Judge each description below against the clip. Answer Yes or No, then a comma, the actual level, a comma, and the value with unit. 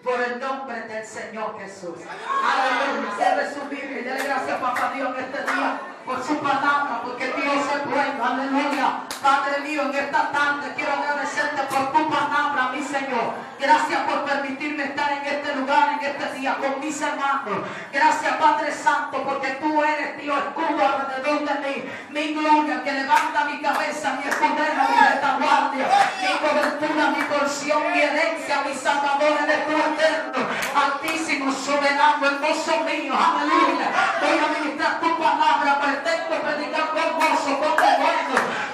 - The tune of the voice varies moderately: No, narrow, 1.6 semitones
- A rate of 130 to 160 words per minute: Yes, average, 155 wpm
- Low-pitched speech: No, very high, 285 Hz